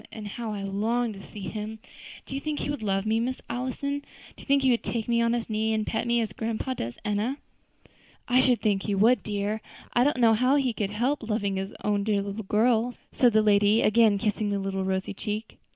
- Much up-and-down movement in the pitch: No, average, 2.9 semitones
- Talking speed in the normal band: No, fast, 230 wpm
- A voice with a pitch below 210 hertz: No, high, 220 Hz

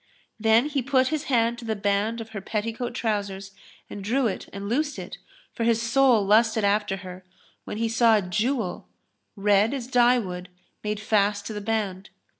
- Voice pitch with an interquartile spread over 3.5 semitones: No, average, 2.8 semitones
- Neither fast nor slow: Yes, average, 190 wpm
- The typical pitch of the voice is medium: No, high, 220 Hz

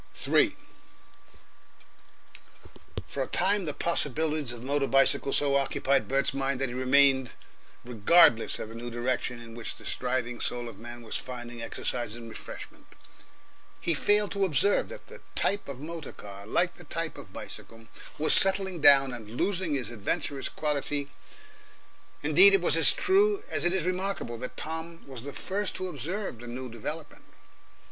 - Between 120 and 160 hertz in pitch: Yes, medium, 140 Hz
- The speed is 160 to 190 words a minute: Yes, average, 165 wpm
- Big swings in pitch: Yes, wide, 5.9 semitones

